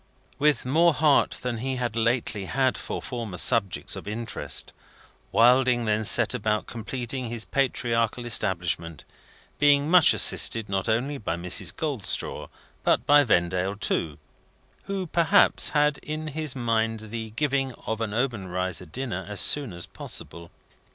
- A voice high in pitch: No, low, 115 Hz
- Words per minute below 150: Yes, average, 140 wpm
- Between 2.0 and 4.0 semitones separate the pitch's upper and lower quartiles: No, average, 4.8 semitones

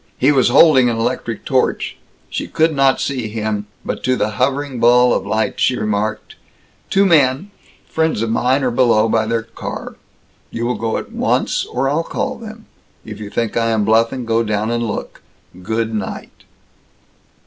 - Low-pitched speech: Yes, low, 115 Hz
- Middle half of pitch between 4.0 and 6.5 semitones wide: No, average, 3.4 semitones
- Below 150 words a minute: No, average, 175 wpm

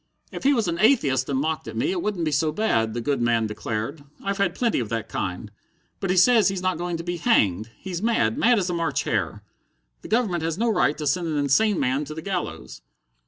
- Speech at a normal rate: No, fast, 240 wpm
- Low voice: No, medium, 165 Hz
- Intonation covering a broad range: Yes, wide, 7.0 semitones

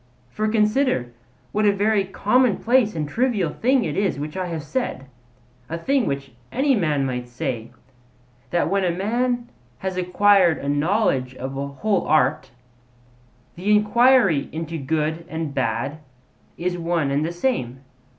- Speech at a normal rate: Yes, average, 150 wpm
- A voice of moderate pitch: Yes, medium, 175 Hz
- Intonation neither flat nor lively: No, wide, 6.6 semitones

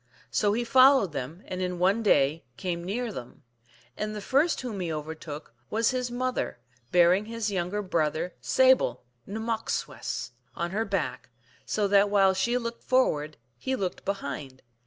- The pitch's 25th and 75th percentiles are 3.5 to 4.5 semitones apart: No, wide, 5.6 semitones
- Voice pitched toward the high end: Yes, high, 195 Hz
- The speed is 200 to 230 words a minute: No, average, 165 wpm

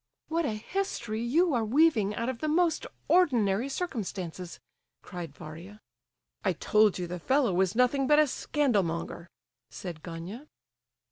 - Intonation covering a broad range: Yes, wide, 8.1 semitones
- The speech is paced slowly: No, average, 145 wpm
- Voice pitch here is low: No, high, 220 Hz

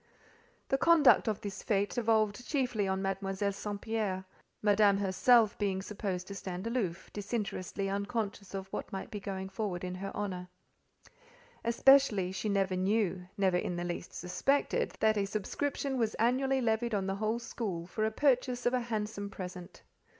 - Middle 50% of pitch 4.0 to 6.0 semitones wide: No, average, 3.2 semitones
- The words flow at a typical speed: Yes, average, 165 wpm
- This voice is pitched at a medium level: No, high, 205 Hz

